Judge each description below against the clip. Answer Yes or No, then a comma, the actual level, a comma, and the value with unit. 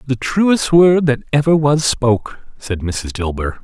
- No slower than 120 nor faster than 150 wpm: No, average, 180 wpm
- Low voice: Yes, low, 130 Hz